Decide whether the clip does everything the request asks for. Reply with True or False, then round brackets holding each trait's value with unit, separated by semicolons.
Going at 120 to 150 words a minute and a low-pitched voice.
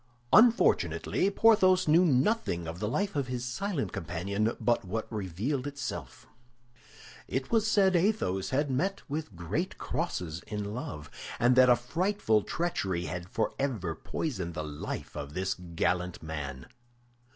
True (140 wpm; 120 Hz)